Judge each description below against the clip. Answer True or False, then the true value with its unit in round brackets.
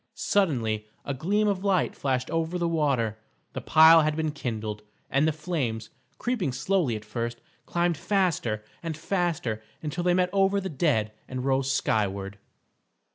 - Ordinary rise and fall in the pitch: False (7.0 semitones)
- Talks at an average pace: True (155 wpm)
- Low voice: False (150 Hz)